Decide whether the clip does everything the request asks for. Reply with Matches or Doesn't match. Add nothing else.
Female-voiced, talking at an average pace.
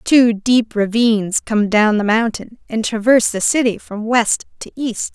Matches